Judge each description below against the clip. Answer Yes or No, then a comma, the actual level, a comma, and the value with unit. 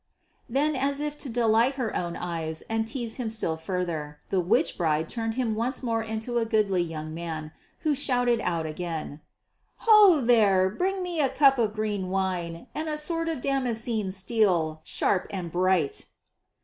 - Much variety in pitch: Yes, wide, 6.7 semitones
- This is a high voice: Yes, high, 220 Hz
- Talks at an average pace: Yes, average, 170 wpm